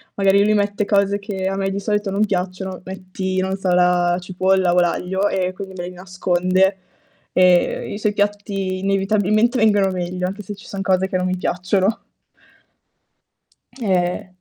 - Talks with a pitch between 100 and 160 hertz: No, high, 190 Hz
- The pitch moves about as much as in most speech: No, narrow, 1.6 semitones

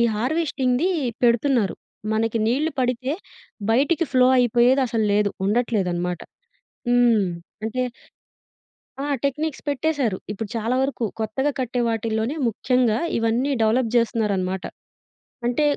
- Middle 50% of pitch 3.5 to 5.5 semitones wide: No, average, 2.9 semitones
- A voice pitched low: No, high, 240 Hz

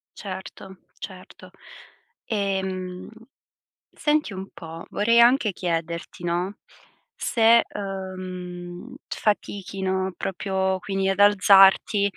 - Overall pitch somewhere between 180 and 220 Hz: Yes, high, 190 Hz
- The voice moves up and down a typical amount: No, narrow, 1.7 semitones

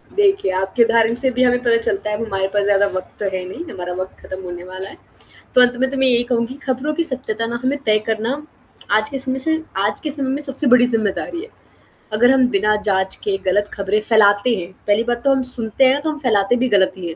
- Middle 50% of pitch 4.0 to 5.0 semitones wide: Yes, average, 4.7 semitones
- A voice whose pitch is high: Yes, high, 230 Hz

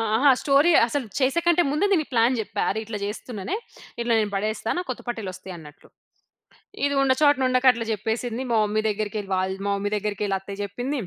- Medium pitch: No, high, 225 Hz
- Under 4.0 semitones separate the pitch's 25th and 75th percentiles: No, average, 4.6 semitones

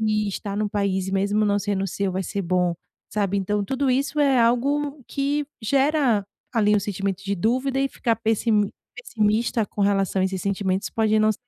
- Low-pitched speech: No, high, 210 Hz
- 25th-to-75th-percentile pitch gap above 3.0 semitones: Yes, average, 3.8 semitones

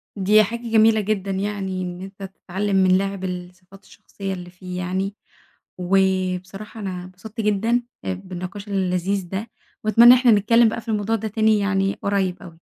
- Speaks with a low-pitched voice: No, high, 195 Hz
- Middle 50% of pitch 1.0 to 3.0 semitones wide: Yes, narrow, 2.4 semitones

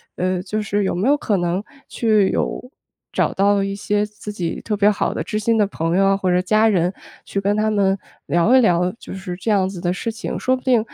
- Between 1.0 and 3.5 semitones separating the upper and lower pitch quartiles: Yes, narrow, 2.6 semitones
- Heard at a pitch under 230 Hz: Yes, high, 200 Hz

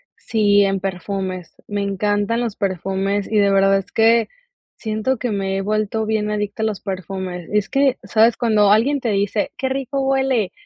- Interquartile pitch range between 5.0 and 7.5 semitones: No, narrow, 2.5 semitones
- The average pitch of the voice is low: No, high, 205 Hz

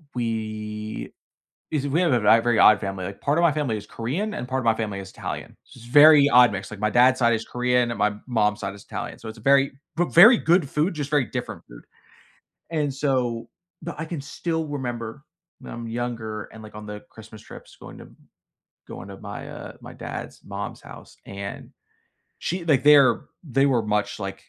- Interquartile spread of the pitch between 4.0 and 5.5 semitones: Yes, average, 5.0 semitones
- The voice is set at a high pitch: No, low, 120 Hz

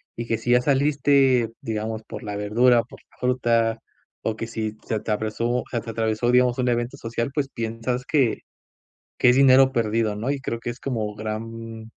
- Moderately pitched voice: No, low, 115 Hz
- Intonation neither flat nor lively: No, narrow, 2.2 semitones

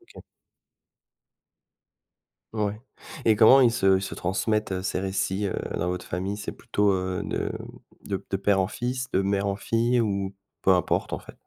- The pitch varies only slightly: Yes, narrow, 2.2 semitones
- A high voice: No, low, 100 Hz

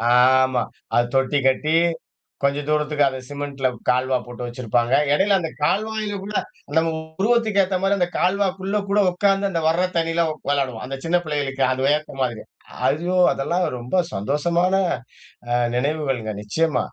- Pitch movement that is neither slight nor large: No, wide, 5.8 semitones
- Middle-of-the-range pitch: Yes, medium, 150 Hz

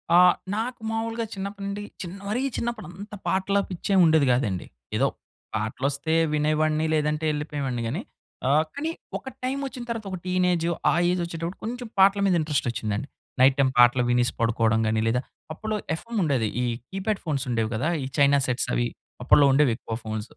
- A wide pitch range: Yes, wide, 7.7 semitones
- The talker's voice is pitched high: No, medium, 155 Hz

